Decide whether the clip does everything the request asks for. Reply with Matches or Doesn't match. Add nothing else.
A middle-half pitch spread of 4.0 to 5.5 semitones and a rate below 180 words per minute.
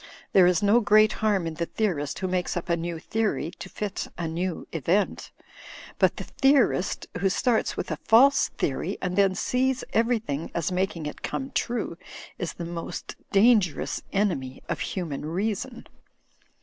Matches